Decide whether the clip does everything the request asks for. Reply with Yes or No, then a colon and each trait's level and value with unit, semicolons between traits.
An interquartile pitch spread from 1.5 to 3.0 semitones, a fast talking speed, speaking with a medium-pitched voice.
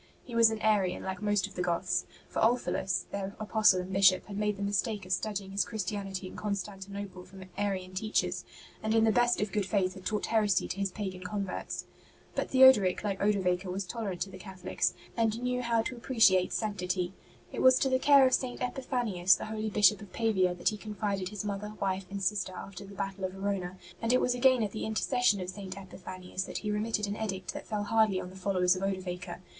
No: narrow, 2.6 semitones; fast, 225 wpm; high, 200 Hz